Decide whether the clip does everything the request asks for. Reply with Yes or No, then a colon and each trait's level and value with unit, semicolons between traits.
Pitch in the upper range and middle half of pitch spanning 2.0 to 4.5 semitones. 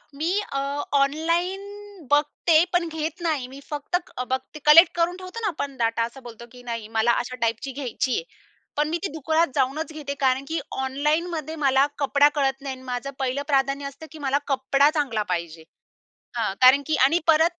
Yes: very high, 280 Hz; average, 3.6 semitones